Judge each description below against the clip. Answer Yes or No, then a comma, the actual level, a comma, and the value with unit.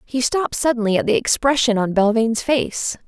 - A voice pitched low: No, high, 240 Hz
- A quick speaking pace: No, average, 175 wpm